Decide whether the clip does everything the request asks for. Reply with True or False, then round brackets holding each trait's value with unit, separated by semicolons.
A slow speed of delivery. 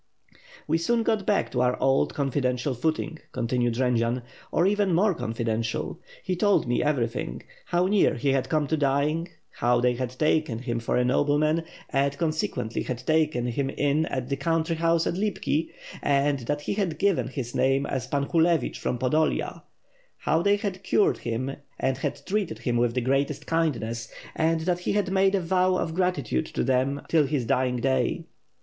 False (180 wpm)